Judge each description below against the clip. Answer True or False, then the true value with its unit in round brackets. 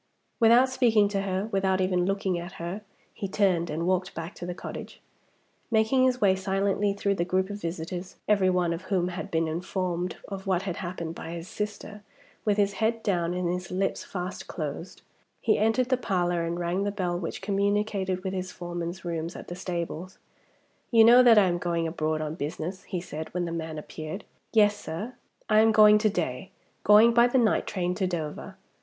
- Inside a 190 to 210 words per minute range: True (200 wpm)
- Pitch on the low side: False (185 Hz)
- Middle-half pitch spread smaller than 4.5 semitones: True (3.0 semitones)